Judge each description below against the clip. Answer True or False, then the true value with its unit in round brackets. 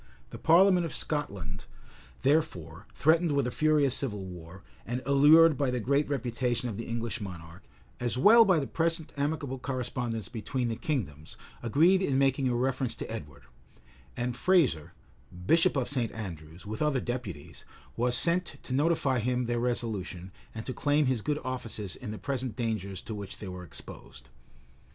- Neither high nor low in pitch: False (125 Hz)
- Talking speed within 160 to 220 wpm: True (170 wpm)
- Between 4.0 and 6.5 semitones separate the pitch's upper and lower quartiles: True (5.2 semitones)